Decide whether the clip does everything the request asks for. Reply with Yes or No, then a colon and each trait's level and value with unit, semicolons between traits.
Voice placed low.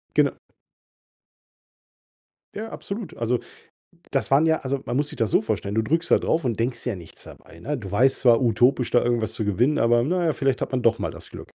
Yes: low, 125 Hz